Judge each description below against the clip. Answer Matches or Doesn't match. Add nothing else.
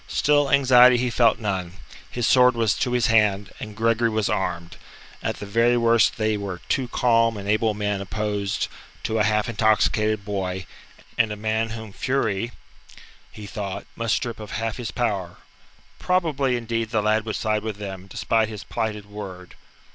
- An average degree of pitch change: Doesn't match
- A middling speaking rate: Matches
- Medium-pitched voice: Doesn't match